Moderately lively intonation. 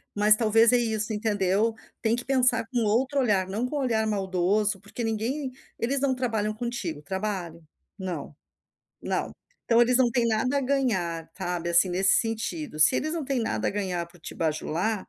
Yes: average, 4.5 semitones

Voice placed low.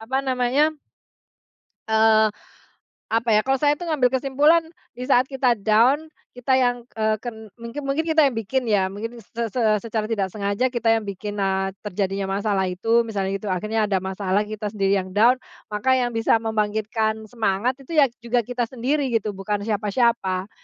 No: high, 225 Hz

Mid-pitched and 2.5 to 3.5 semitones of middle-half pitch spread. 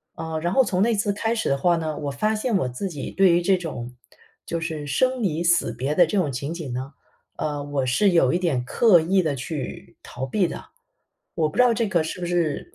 No: medium, 165 Hz; average, 5.2 semitones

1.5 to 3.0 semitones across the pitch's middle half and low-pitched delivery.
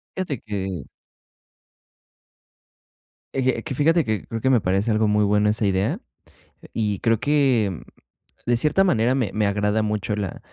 No: average, 4.0 semitones; low, 110 Hz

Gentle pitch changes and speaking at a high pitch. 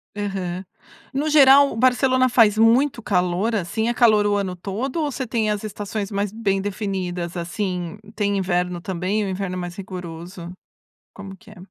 No: average, 3.7 semitones; high, 200 Hz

